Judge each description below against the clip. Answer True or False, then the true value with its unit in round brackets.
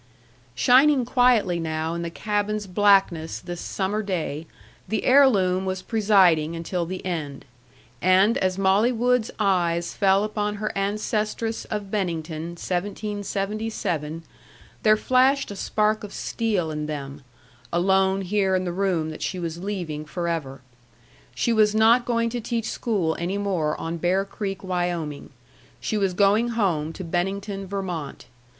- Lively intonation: False (3.8 semitones)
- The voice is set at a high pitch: True (195 Hz)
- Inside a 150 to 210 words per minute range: False (140 wpm)